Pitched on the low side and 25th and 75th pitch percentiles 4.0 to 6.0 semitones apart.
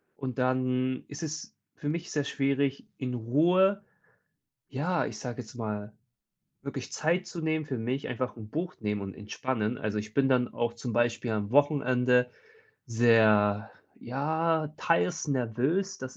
Yes: low, 130 Hz; average, 4.4 semitones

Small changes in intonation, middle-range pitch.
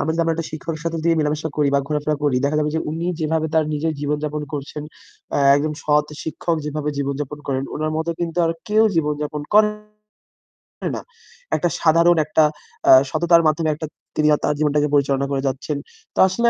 Yes: narrow, 1.7 semitones; medium, 155 Hz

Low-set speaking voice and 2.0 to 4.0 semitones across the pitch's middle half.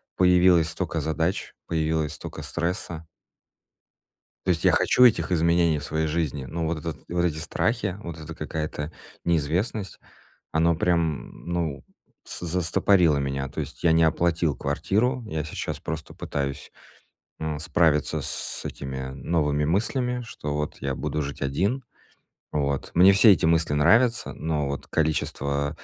Yes: very low, 80 Hz; average, 2.9 semitones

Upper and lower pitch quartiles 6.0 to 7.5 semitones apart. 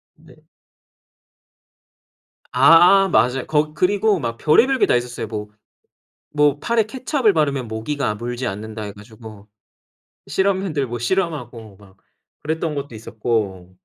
Yes: wide, 7.0 semitones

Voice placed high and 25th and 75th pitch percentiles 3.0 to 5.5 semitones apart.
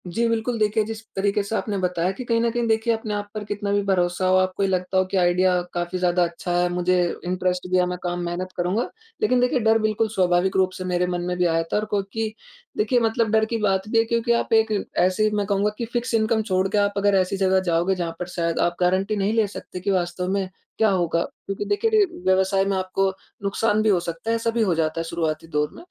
Yes: high, 195 Hz; average, 3.4 semitones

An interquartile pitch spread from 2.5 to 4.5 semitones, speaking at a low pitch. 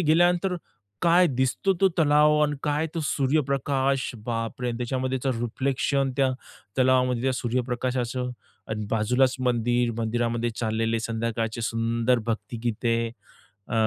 Yes: average, 2.8 semitones; low, 125 Hz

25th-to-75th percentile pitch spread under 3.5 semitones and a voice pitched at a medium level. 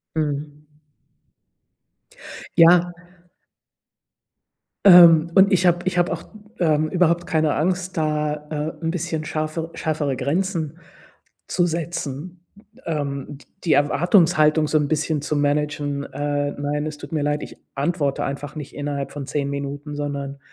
Yes: average, 2.7 semitones; medium, 155 Hz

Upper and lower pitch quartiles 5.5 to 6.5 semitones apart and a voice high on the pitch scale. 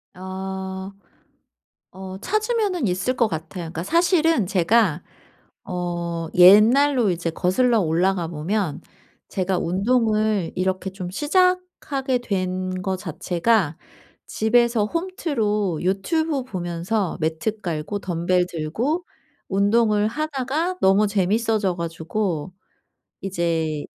No: average, 5.1 semitones; high, 195 Hz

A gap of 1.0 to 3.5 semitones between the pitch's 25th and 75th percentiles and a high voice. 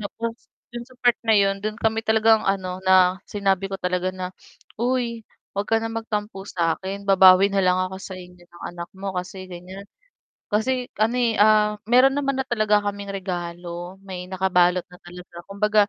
Yes: average, 3.1 semitones; high, 195 Hz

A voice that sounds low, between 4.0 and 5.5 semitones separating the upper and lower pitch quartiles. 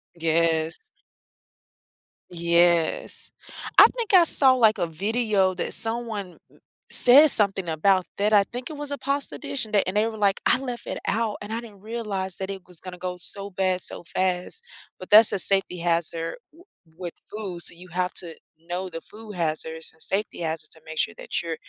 No: high, 190 Hz; average, 4.3 semitones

